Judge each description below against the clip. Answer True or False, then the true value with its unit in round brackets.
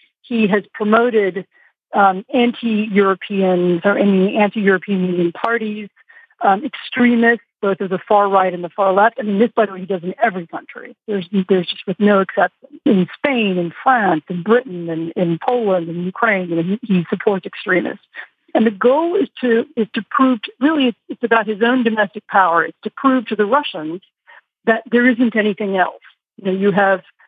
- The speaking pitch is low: False (210 Hz)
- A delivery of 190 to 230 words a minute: True (195 wpm)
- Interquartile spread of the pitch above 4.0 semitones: False (3.7 semitones)